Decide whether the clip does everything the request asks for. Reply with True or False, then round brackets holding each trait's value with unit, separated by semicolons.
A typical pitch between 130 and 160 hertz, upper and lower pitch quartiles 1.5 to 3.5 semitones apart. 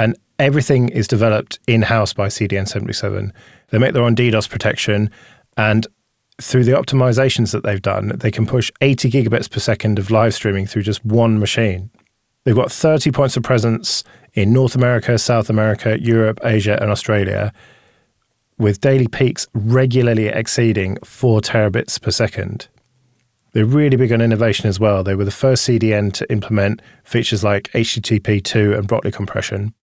False (110 Hz; 2.6 semitones)